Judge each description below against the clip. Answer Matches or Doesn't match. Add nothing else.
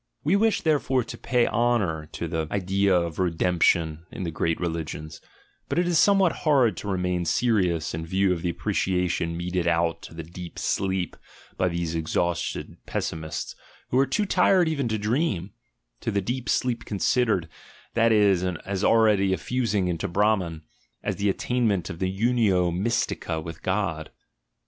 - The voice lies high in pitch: Doesn't match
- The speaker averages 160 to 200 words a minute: Matches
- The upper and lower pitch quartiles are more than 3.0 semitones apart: Matches